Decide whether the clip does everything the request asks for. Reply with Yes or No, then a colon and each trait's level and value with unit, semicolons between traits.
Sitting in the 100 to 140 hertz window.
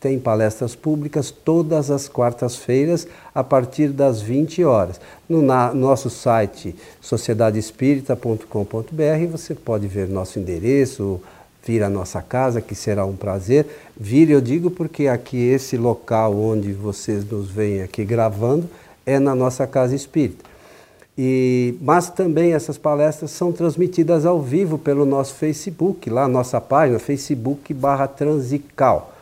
Yes: low, 135 Hz